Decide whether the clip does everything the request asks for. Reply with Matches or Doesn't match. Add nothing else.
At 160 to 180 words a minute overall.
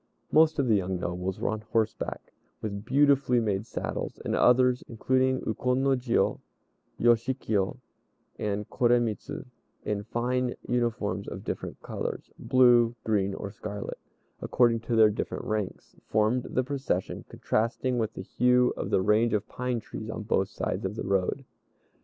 Doesn't match